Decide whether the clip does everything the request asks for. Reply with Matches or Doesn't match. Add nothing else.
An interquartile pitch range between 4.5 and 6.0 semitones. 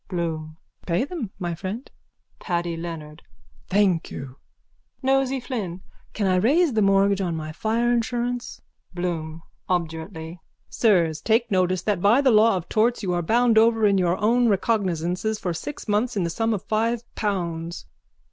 Matches